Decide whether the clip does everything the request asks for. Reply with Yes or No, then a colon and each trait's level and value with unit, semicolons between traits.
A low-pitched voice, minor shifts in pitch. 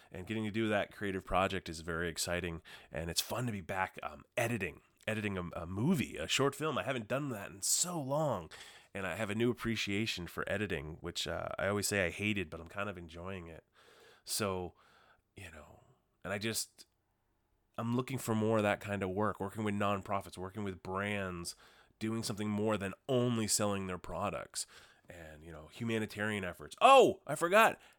No: low, 100 Hz; average, 3.4 semitones